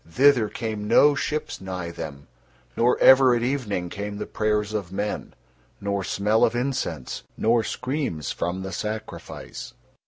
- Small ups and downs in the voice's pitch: No, average, 4.3 semitones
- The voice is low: Yes, low, 105 Hz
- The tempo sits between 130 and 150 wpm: Yes, average, 145 wpm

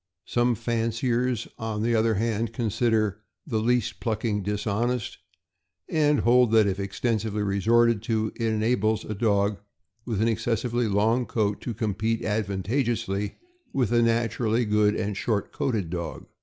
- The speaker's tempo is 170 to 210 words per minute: No, average, 140 wpm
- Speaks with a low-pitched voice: Yes, low, 110 Hz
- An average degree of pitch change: No, narrow, 2.2 semitones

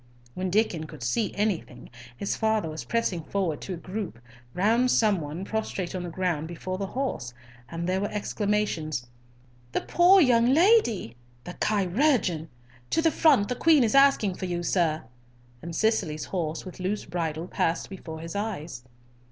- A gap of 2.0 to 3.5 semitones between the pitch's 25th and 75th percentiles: No, average, 4.9 semitones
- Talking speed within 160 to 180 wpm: Yes, average, 165 wpm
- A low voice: No, high, 190 Hz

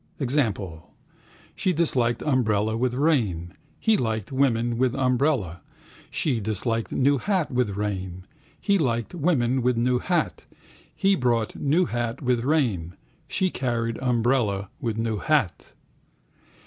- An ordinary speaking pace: No, slow, 125 wpm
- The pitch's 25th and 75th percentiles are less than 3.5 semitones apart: No, average, 4.1 semitones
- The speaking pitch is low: Yes, low, 120 Hz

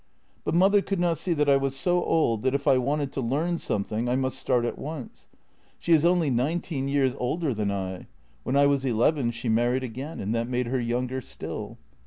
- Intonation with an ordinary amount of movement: Yes, average, 4.1 semitones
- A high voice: No, low, 135 Hz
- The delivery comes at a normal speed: No, fast, 225 wpm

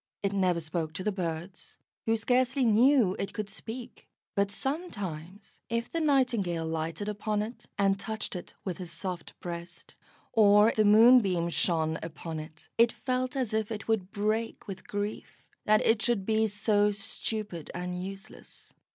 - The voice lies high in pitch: Yes, high, 205 Hz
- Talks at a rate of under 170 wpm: Yes, average, 160 wpm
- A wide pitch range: No, average, 3.9 semitones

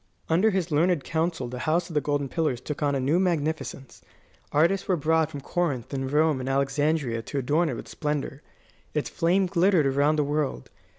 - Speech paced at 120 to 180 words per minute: No, average, 190 wpm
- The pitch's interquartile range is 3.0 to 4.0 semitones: Yes, average, 3.3 semitones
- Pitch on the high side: No, medium, 150 Hz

